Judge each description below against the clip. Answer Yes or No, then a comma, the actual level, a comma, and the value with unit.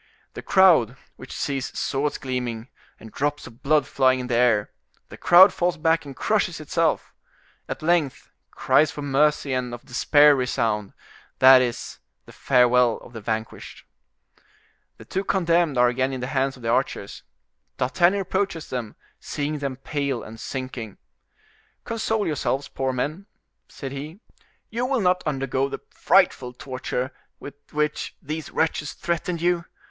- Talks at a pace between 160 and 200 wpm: No, average, 150 wpm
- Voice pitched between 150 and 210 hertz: No, low, 135 Hz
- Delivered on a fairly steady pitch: No, average, 4.2 semitones